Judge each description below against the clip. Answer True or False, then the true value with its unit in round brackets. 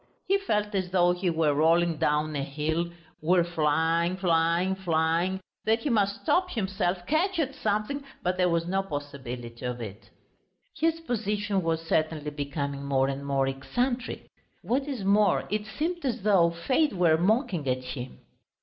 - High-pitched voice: False (175 Hz)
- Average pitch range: False (5.8 semitones)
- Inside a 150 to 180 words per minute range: True (160 wpm)